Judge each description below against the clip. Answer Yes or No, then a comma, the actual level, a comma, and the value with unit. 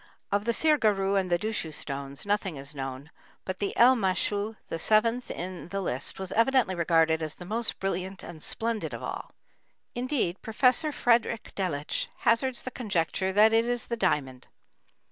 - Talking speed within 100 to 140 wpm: No, average, 160 wpm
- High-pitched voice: Yes, high, 195 Hz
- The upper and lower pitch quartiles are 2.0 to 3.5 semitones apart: No, average, 5.3 semitones